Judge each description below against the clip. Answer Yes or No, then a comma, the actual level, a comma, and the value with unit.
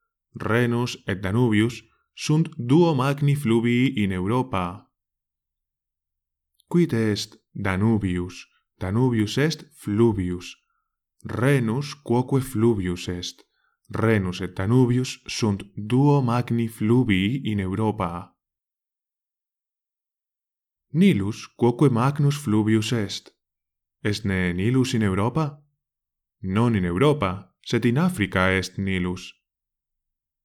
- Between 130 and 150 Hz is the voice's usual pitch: No, low, 110 Hz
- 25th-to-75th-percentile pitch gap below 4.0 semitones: No, average, 5.1 semitones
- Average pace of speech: No, slow, 90 wpm